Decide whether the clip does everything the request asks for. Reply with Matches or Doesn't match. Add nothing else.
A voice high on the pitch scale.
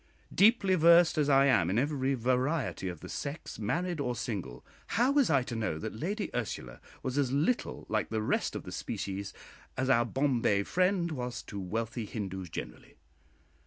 Doesn't match